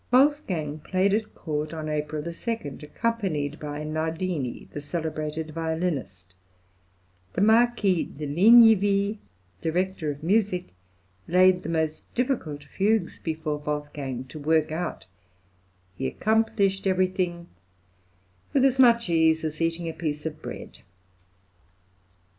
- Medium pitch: Yes, medium, 165 Hz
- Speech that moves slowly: Yes, slow, 115 wpm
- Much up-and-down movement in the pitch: No, average, 4.5 semitones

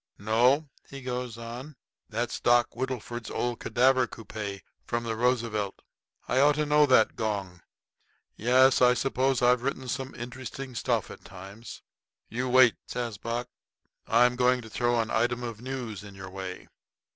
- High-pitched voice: No, low, 120 Hz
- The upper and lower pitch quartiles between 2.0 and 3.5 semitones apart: Yes, narrow, 2.4 semitones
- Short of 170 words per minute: Yes, average, 155 wpm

